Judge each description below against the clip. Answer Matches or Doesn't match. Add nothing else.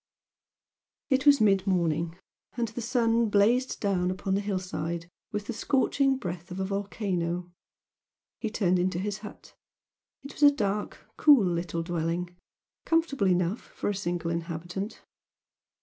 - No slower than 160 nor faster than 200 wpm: Doesn't match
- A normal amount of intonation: Matches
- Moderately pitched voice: Doesn't match